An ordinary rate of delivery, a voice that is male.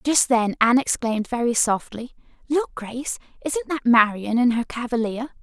No: average, 155 wpm; female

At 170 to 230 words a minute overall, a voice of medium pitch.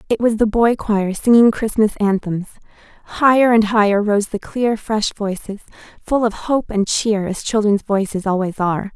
No: average, 175 wpm; high, 210 Hz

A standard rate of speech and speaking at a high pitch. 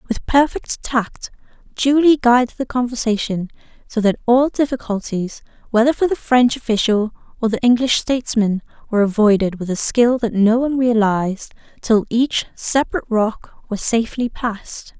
Yes: average, 145 wpm; high, 230 Hz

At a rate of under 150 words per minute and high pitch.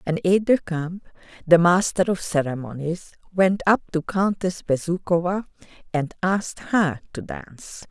No: slow, 135 wpm; medium, 175 Hz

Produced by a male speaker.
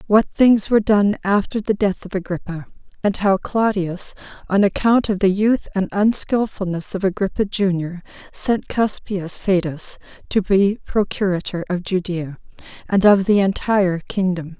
No: female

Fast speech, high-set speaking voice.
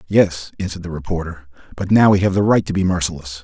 No: fast, 225 wpm; very low, 90 Hz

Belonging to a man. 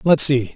Yes: male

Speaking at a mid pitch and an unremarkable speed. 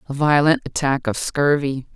Yes: medium, 145 Hz; average, 155 wpm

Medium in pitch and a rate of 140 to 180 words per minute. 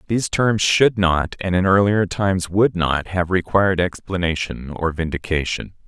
No: very low, 90 Hz; average, 155 wpm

